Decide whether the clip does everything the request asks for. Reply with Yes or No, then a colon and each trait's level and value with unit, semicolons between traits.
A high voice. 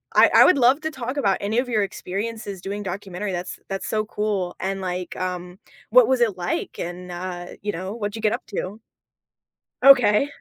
Yes: high, 200 Hz